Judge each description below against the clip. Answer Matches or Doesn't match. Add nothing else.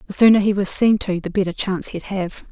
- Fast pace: Matches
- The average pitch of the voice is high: Matches